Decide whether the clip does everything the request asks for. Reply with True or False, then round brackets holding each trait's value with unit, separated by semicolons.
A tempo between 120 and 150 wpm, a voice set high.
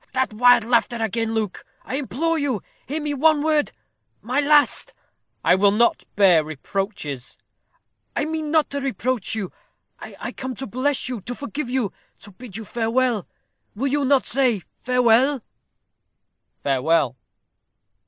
True (145 wpm; 245 Hz)